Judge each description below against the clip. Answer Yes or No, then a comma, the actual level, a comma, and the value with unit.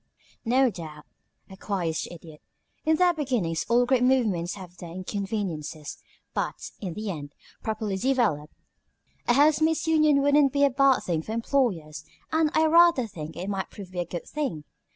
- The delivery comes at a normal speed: Yes, average, 160 wpm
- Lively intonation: Yes, wide, 8.1 semitones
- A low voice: No, high, 215 Hz